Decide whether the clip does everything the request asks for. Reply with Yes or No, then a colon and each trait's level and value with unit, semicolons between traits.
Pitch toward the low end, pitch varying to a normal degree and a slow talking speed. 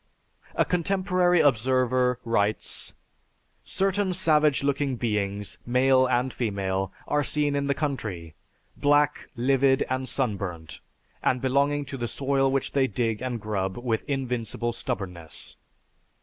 Yes: low, 130 Hz; average, 4.4 semitones; slow, 120 wpm